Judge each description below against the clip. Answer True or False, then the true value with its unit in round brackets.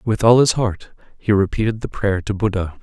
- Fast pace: True (210 wpm)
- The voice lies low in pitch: True (105 Hz)